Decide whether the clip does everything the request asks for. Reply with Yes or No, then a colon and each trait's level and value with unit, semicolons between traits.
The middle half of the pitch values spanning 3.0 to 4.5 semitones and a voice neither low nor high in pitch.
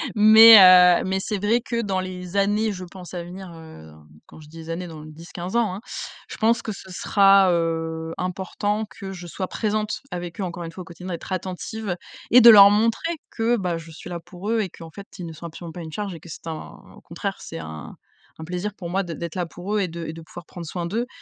Yes: average, 3.5 semitones; medium, 180 Hz